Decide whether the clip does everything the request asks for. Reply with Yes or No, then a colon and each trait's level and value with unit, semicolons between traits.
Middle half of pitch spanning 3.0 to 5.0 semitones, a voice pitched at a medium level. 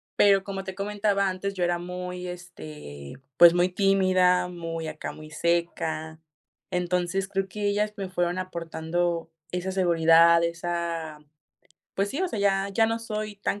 No: narrow, 2.6 semitones; medium, 180 Hz